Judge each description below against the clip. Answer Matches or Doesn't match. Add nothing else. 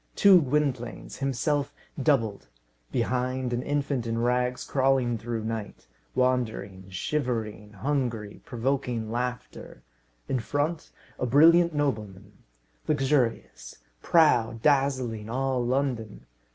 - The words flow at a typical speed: Doesn't match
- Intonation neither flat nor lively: Matches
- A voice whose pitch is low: Matches